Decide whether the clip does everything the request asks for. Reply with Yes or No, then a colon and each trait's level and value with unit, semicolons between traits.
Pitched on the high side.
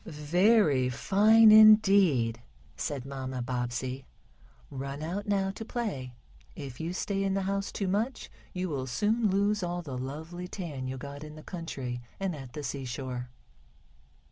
No: medium, 155 Hz